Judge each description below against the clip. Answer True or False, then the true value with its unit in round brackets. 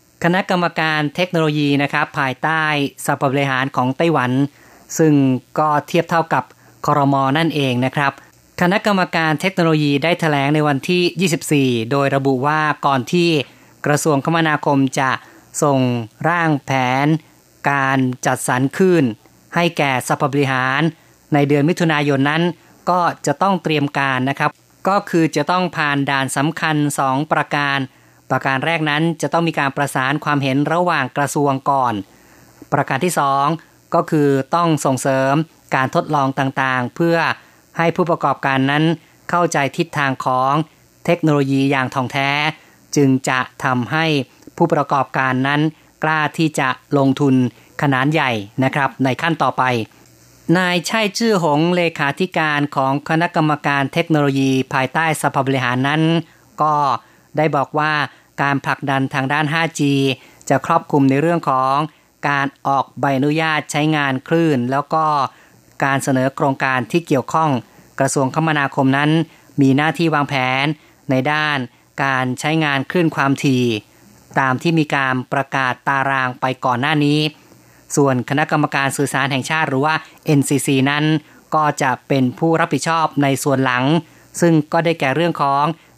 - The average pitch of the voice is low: False (145 Hz)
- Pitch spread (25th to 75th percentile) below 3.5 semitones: True (2.9 semitones)